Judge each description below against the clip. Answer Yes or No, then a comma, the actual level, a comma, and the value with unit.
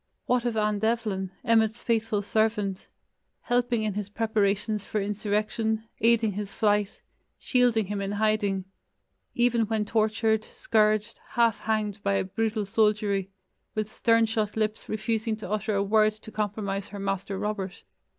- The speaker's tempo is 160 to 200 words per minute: No, average, 145 wpm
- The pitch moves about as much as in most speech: No, narrow, 1.6 semitones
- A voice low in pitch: No, high, 215 Hz